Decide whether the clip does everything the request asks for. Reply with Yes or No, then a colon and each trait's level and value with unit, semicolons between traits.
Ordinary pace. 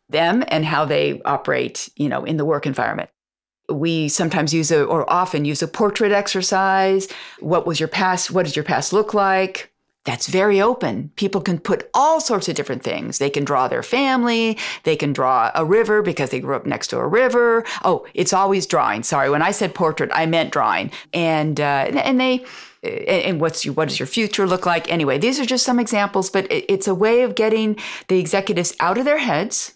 No: fast, 210 wpm